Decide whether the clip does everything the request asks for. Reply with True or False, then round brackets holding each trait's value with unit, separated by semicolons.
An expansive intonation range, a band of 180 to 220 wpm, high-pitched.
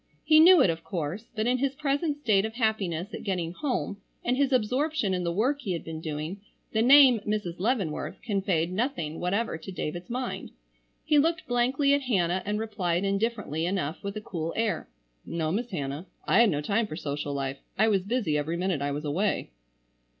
True (6.4 semitones; 195 wpm; 200 Hz)